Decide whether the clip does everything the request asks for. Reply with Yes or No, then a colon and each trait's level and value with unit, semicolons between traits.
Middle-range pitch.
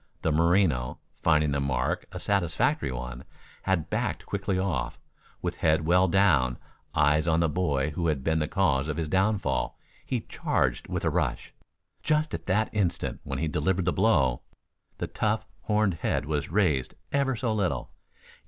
No: very low, 80 Hz